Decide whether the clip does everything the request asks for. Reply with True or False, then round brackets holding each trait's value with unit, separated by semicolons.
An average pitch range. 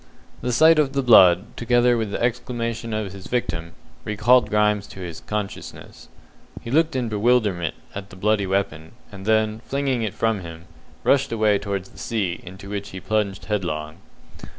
True (3.7 semitones)